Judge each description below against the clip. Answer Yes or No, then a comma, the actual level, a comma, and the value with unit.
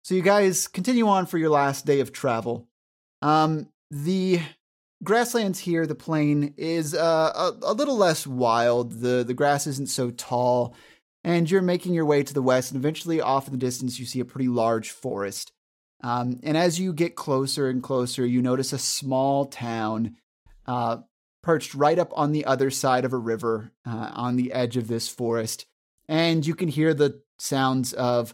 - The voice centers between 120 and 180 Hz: Yes, low, 135 Hz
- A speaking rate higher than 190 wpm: No, average, 185 wpm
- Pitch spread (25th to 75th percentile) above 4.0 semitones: Yes, average, 4.7 semitones